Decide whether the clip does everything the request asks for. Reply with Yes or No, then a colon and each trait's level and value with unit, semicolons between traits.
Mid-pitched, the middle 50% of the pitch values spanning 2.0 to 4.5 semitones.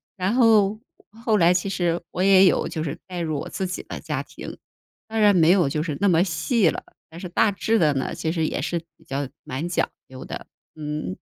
Yes: medium, 175 Hz; average, 4.1 semitones